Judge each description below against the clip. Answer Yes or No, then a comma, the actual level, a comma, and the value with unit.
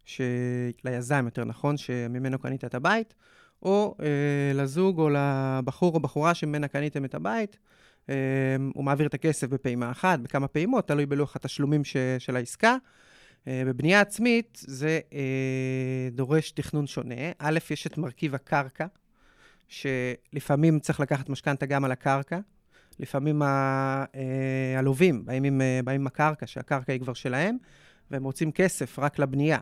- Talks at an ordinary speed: Yes, average, 140 wpm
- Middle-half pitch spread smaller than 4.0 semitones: Yes, average, 2.9 semitones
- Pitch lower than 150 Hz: Yes, medium, 140 Hz